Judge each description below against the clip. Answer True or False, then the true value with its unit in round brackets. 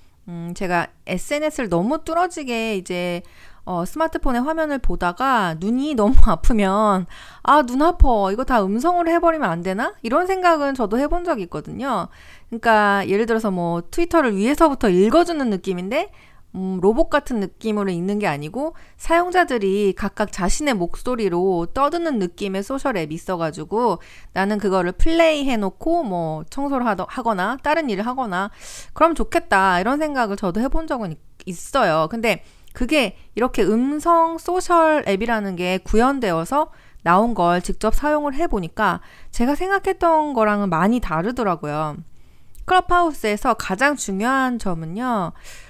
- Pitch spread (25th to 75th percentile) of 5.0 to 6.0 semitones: False (7.7 semitones)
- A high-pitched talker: True (225 Hz)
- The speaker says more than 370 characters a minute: False (325 characters per minute)